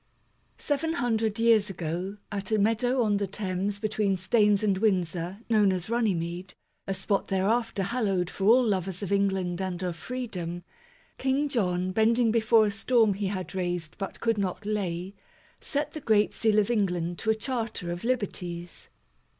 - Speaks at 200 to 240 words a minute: No, average, 165 wpm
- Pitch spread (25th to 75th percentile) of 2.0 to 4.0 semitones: Yes, average, 3.5 semitones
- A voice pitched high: Yes, high, 200 Hz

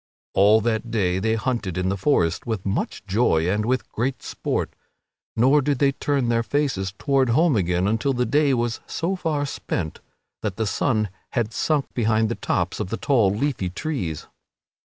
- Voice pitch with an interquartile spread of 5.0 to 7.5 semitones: Yes, wide, 5.5 semitones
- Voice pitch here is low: Yes, low, 115 Hz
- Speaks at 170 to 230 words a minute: Yes, average, 175 wpm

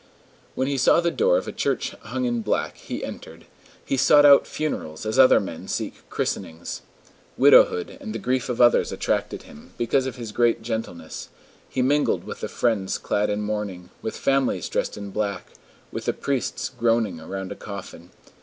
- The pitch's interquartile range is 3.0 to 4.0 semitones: No, average, 5.3 semitones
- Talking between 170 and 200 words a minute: Yes, average, 180 wpm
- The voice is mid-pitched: No, low, 115 Hz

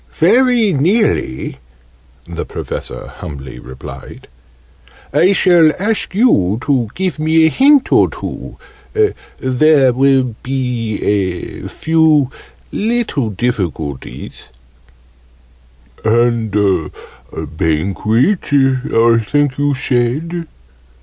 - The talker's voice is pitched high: No, low, 130 Hz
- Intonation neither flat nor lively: No, wide, 7.9 semitones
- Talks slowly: Yes, slow, 90 wpm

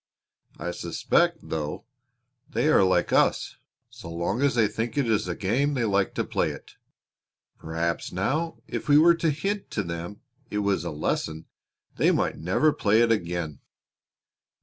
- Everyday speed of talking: Yes, average, 165 wpm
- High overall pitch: No, low, 100 Hz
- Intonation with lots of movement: Yes, wide, 8.1 semitones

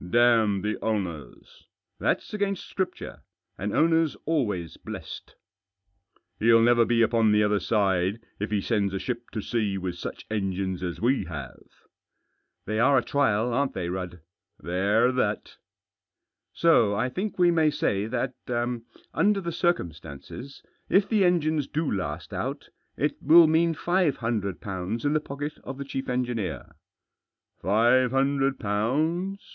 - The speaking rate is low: No, average, 160 wpm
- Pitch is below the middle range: Yes, low, 115 Hz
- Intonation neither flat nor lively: No, wide, 6.6 semitones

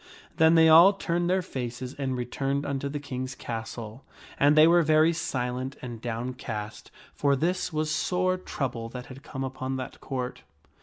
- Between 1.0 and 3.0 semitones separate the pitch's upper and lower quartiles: No, average, 4.1 semitones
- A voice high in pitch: No, low, 135 Hz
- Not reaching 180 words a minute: Yes, average, 170 wpm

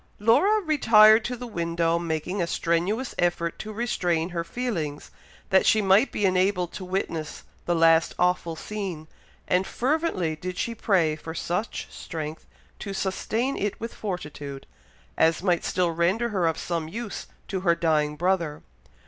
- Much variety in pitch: No, average, 4.3 semitones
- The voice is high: No, medium, 180 Hz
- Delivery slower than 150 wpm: No, average, 155 wpm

